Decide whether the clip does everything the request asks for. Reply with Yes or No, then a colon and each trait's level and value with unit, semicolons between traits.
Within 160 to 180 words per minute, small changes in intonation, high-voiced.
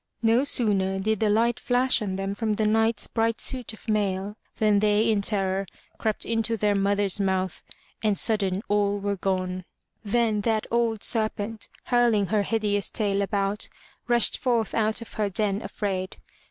Yes: average, 165 wpm; narrow, 2.1 semitones; high, 210 Hz